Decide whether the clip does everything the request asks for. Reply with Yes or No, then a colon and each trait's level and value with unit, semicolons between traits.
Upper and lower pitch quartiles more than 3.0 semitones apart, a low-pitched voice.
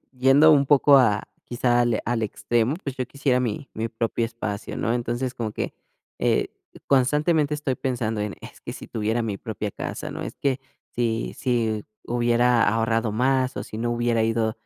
No: narrow, 2.5 semitones; low, 120 Hz